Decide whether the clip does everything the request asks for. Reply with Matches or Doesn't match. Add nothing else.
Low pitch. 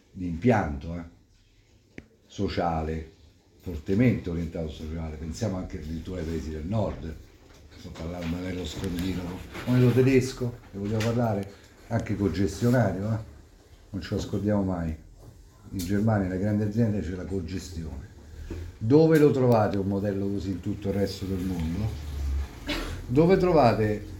Matches